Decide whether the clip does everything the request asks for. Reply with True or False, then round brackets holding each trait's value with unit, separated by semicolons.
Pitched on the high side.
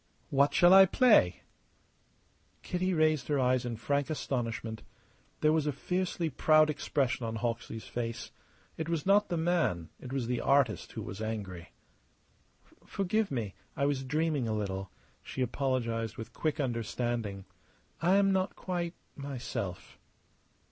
False (135 Hz)